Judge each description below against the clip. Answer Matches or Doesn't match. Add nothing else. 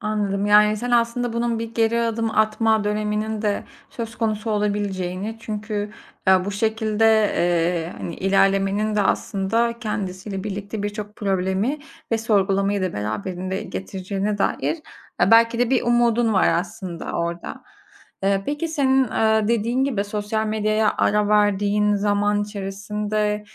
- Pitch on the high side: Matches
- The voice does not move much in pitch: Matches